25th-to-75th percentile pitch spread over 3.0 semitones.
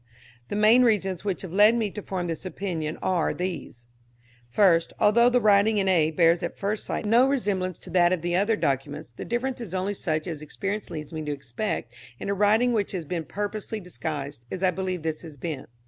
Yes: average, 4.5 semitones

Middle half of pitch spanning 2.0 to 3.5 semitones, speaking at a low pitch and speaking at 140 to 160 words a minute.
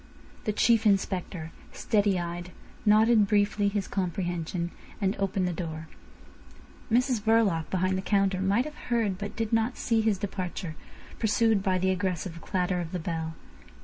No: average, 3.2 semitones; high, 195 Hz; average, 150 wpm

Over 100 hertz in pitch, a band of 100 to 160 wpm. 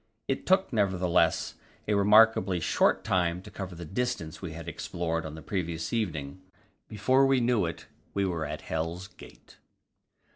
No: very low, 90 Hz; average, 155 wpm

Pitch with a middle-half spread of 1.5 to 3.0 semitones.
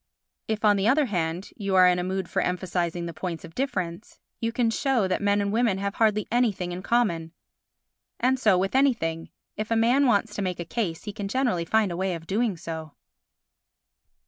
No: average, 4.3 semitones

